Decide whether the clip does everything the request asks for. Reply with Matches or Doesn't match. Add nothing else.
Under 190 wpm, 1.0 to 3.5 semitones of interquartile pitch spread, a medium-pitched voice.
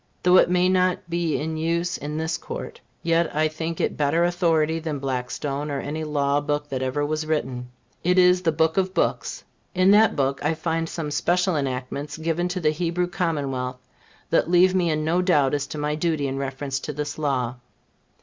Doesn't match